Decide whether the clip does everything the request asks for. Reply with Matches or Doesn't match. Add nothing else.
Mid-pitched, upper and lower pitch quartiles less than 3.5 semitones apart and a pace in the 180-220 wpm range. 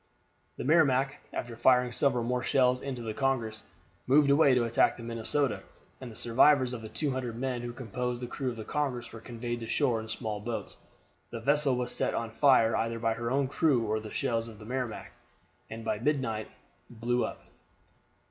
Doesn't match